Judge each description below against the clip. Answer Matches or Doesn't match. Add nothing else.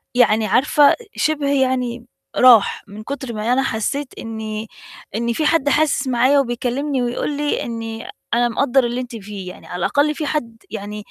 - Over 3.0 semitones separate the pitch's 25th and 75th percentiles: Matches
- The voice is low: Doesn't match